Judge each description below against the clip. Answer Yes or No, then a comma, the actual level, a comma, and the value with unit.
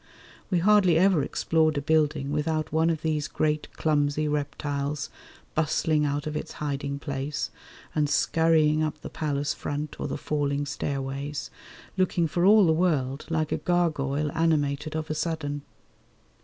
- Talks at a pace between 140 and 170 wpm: Yes, average, 150 wpm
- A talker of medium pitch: Yes, medium, 150 Hz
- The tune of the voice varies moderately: No, narrow, 1.9 semitones